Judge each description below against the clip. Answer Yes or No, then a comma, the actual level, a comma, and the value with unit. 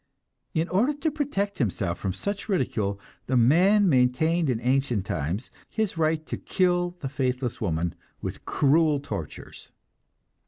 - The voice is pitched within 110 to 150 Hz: Yes, medium, 140 Hz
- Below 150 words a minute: Yes, slow, 135 wpm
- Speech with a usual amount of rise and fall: No, wide, 7.6 semitones